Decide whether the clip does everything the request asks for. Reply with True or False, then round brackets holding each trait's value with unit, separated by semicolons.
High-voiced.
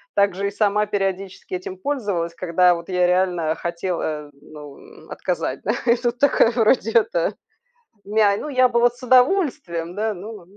True (200 Hz)